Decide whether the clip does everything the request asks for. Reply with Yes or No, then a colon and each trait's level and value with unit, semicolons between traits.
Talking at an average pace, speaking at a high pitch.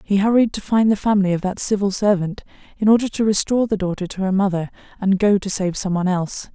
No: fast, 230 wpm; high, 200 Hz